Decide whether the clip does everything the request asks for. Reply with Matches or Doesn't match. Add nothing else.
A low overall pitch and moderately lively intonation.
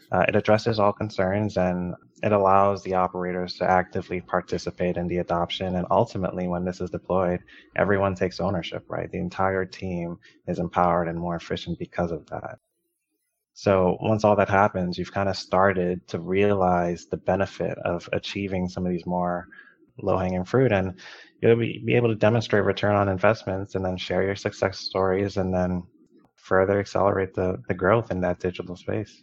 Doesn't match